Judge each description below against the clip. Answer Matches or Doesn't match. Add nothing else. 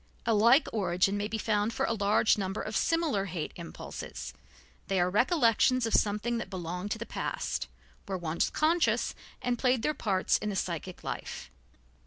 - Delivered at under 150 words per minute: Doesn't match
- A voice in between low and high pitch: Doesn't match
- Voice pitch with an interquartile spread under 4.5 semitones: Matches